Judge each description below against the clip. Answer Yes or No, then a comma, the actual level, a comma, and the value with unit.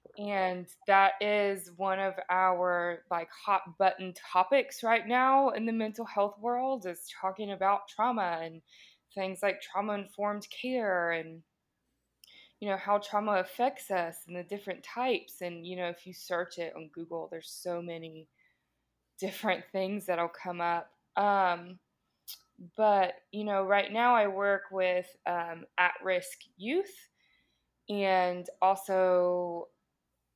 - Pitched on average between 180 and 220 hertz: Yes, high, 190 Hz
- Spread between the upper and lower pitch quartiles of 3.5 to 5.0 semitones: No, average, 2.7 semitones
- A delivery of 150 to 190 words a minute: No, average, 140 wpm